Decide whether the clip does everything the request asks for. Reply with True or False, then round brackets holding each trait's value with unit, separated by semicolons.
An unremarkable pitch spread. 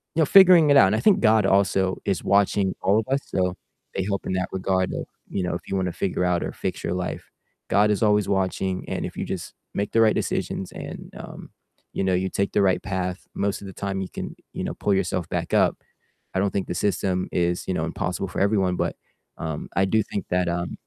False (1.8 semitones)